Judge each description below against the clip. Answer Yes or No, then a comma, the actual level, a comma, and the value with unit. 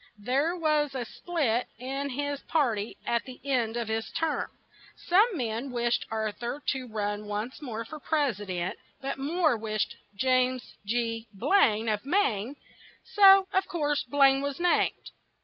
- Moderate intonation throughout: Yes, average, 4.7 semitones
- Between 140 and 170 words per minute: Yes, average, 160 wpm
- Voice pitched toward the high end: Yes, very high, 255 Hz